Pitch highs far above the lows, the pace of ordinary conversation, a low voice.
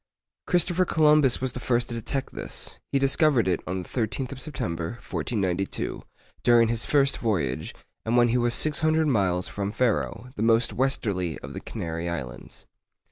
Yes: wide, 6.0 semitones; average, 170 wpm; low, 120 Hz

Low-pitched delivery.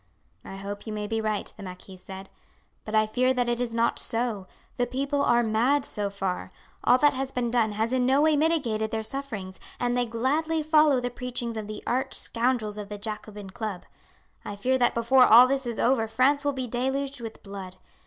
No: high, 235 Hz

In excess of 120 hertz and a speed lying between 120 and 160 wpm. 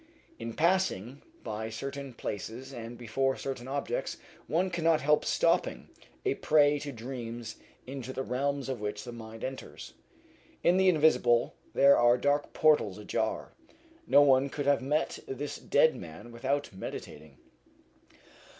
Yes: low, 135 Hz; average, 140 wpm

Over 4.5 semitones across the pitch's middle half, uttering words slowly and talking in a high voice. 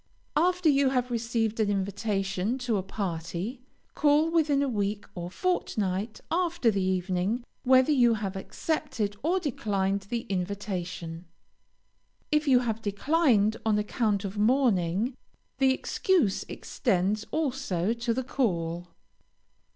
Yes: wide, 5.4 semitones; slow, 125 wpm; high, 220 Hz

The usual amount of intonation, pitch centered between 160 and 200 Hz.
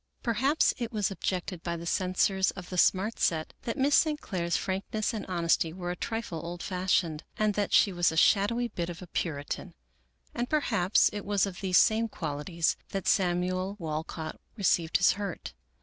Yes: average, 3.4 semitones; medium, 185 Hz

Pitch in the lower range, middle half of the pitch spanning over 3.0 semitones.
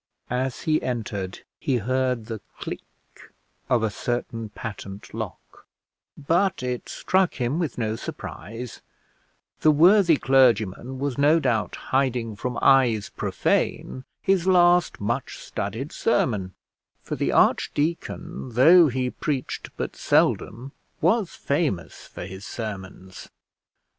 Yes: low, 125 Hz; average, 5.3 semitones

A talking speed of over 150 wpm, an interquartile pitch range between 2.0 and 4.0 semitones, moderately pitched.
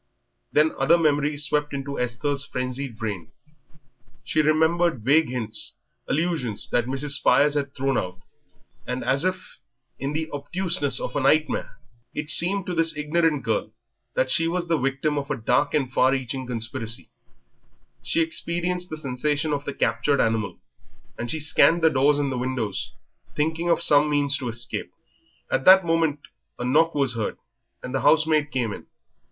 Yes: average, 160 wpm; average, 3.7 semitones; medium, 145 Hz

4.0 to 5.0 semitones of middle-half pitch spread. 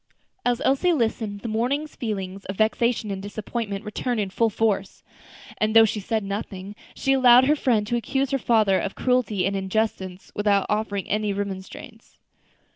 No: average, 3.2 semitones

